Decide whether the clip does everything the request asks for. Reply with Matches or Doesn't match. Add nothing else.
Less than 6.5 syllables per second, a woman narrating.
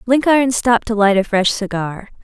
Matches